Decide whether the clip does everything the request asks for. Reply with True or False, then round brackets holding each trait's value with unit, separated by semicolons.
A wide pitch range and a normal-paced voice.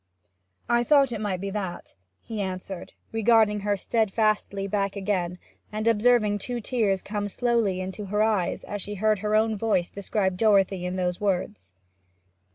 False (2.4 semitones; 160 wpm)